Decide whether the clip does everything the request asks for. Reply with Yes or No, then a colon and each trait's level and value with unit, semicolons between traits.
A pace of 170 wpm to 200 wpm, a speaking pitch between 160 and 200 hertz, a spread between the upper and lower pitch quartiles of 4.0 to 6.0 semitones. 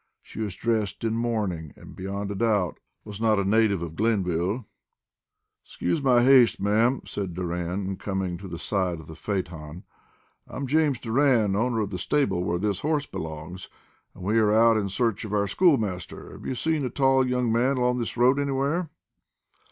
No: average, 180 wpm; low, 105 Hz; average, 4.9 semitones